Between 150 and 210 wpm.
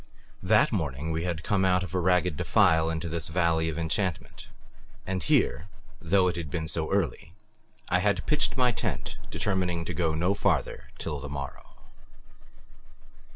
Yes: average, 160 wpm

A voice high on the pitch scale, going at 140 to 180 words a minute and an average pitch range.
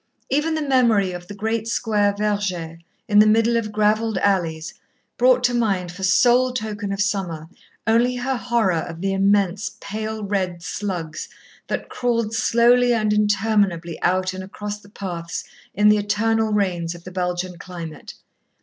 Yes: high, 205 Hz; average, 160 wpm; average, 3.5 semitones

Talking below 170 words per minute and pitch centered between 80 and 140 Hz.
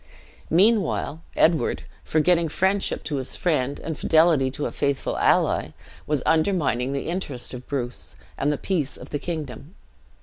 No: average, 145 wpm; medium, 155 Hz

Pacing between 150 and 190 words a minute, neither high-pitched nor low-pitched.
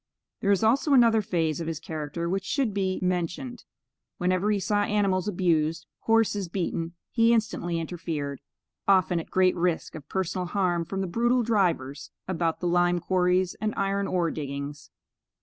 Yes: average, 160 wpm; medium, 180 Hz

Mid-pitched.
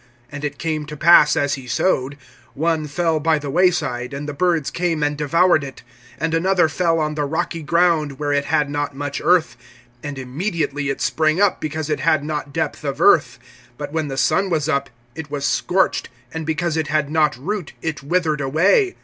Yes: medium, 155 Hz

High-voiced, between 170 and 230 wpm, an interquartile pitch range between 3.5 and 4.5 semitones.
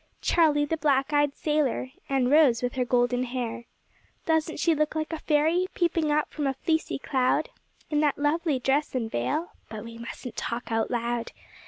Yes: very high, 280 Hz; average, 180 wpm; average, 3.9 semitones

